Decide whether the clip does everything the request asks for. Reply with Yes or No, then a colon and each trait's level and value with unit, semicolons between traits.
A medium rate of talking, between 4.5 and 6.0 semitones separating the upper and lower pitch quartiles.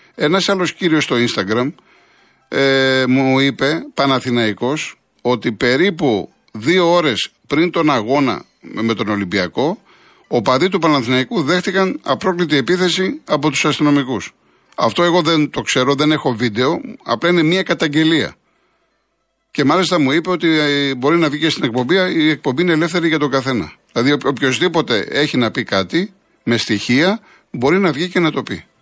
Yes: average, 155 wpm; average, 5.2 semitones